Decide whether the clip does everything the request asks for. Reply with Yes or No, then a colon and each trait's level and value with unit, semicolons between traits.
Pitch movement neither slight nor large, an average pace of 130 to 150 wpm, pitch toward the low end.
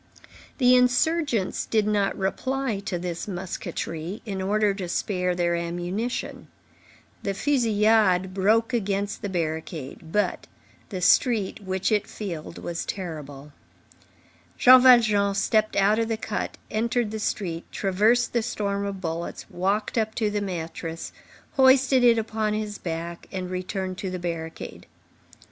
No: average, 3.6 semitones; slow, 135 wpm; high, 200 Hz